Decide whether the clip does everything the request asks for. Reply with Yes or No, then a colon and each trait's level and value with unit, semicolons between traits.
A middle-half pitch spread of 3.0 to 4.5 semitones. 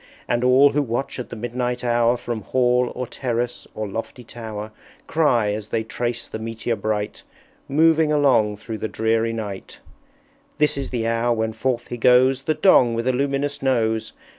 No: narrow, 2.5 semitones